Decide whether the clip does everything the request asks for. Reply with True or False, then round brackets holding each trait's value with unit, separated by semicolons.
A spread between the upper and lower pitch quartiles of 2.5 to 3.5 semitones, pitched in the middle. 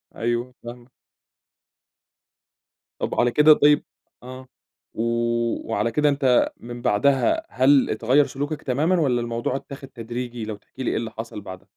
False (3.1 semitones; 125 Hz)